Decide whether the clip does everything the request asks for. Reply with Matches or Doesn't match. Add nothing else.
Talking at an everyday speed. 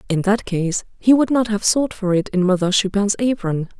Doesn't match